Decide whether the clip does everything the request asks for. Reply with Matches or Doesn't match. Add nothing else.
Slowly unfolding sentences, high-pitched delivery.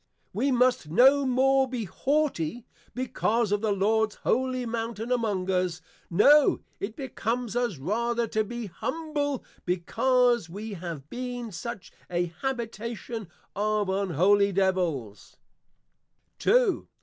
Matches